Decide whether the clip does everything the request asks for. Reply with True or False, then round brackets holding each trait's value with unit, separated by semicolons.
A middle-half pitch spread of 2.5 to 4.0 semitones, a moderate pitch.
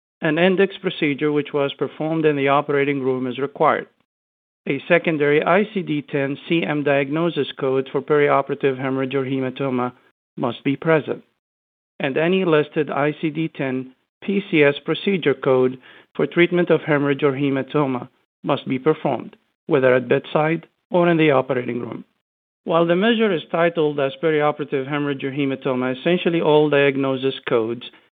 True (3.2 semitones; 145 Hz)